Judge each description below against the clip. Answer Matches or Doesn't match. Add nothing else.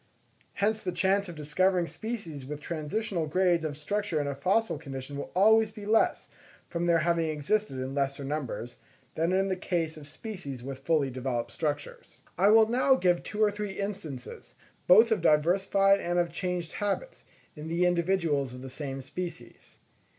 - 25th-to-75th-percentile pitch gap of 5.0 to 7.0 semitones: Matches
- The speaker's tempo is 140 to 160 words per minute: Doesn't match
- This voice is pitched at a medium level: Matches